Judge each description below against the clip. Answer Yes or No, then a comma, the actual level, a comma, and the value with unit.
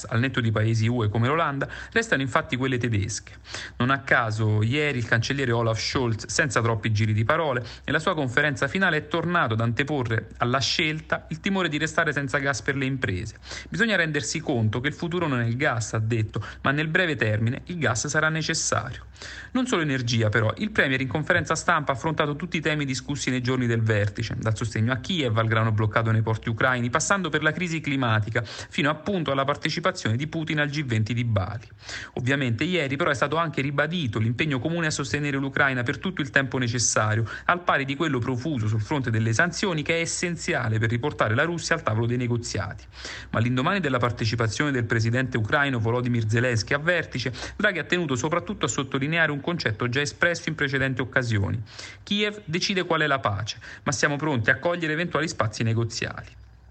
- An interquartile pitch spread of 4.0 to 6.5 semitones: Yes, average, 5.3 semitones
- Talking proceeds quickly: Yes, fast, 195 wpm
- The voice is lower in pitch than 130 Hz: No, low, 135 Hz